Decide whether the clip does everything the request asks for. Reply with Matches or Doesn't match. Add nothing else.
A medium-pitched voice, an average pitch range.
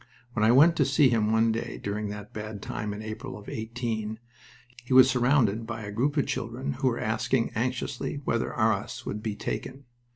Doesn't match